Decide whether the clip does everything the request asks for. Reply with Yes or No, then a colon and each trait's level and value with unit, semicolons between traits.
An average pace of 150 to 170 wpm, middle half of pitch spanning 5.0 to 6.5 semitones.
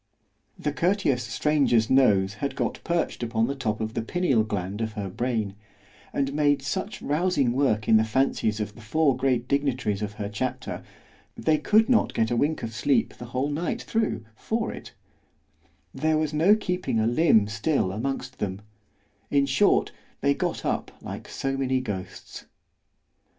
Yes: average, 160 wpm; wide, 5.4 semitones